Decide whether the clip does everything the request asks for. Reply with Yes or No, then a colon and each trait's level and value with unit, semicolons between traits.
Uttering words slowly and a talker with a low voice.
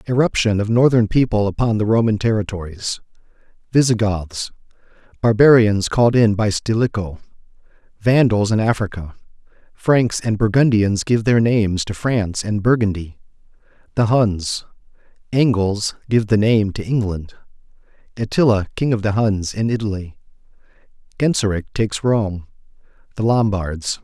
Yes: slow, 95 wpm; low, 110 Hz